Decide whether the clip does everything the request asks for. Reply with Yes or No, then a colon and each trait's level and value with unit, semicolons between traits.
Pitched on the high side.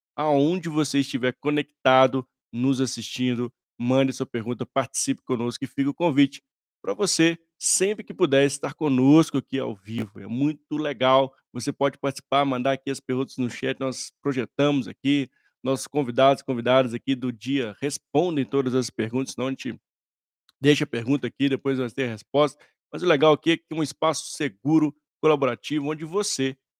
No: low, 135 Hz